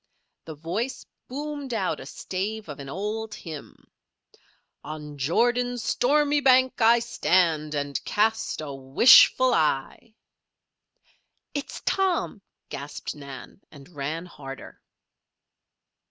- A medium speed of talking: No, slow, 105 wpm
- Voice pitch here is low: No, high, 190 Hz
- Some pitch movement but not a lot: No, wide, 8.7 semitones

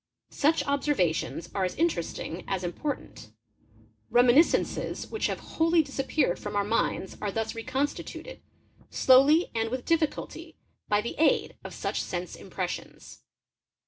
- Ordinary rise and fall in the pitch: No, wide, 6.8 semitones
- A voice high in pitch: Yes, very high, 255 Hz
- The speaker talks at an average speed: No, slow, 130 wpm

